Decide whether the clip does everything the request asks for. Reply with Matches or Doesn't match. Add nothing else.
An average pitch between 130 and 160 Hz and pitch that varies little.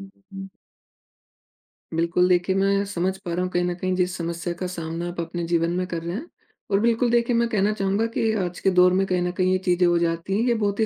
Doesn't match